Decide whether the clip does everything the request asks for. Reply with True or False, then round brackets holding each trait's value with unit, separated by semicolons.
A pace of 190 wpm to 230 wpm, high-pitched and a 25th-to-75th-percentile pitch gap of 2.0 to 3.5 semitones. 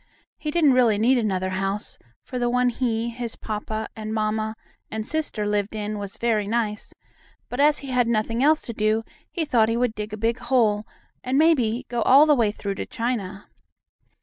True (200 wpm; 225 Hz; 2.8 semitones)